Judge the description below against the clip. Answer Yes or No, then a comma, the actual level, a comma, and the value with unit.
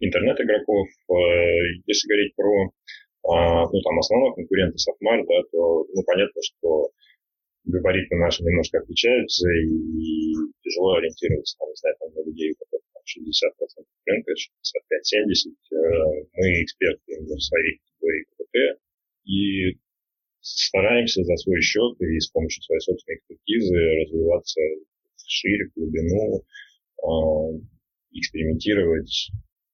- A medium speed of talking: No, slow, 105 wpm